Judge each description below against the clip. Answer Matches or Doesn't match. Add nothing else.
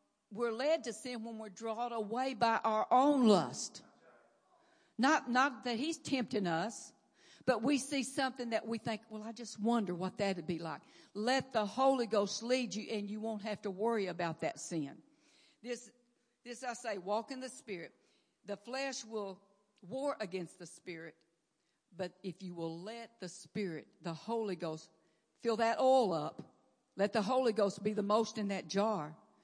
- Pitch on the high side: Matches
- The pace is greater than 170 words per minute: Matches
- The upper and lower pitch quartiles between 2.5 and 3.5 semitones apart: Doesn't match